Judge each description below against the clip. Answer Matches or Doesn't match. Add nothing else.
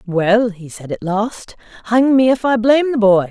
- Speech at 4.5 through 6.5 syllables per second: Matches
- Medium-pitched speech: Doesn't match